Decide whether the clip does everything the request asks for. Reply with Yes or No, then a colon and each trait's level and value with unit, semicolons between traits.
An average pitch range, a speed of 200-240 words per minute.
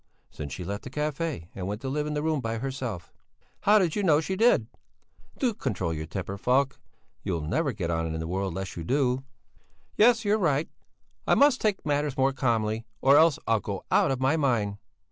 No: wide, 7.5 semitones; fast, 205 wpm